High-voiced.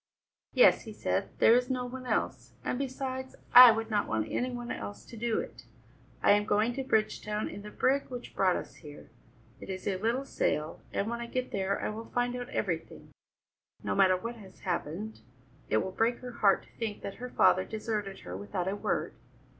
Yes: high, 220 Hz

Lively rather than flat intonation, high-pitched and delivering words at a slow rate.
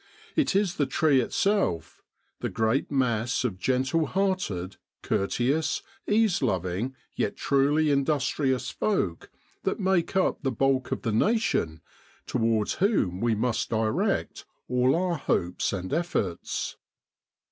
No: wide, 7.5 semitones; low, 130 Hz; slow, 125 wpm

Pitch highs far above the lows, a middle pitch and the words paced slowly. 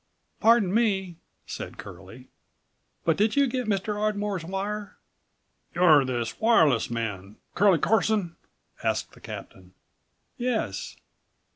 No: wide, 6.7 semitones; high, 195 Hz; slow, 110 wpm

